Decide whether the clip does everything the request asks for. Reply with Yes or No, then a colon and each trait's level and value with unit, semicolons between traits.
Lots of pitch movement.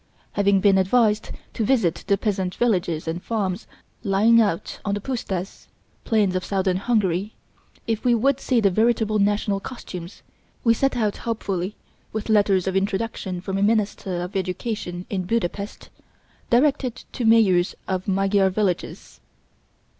No: average, 3.2 semitones